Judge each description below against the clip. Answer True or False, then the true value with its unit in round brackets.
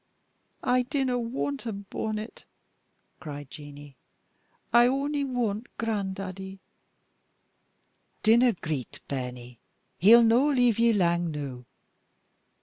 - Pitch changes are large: True (8.0 semitones)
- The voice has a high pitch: True (215 Hz)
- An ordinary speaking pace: False (95 wpm)